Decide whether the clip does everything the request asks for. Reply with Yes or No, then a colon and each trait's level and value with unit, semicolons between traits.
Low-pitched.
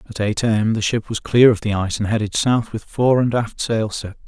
Yes: low, 110 Hz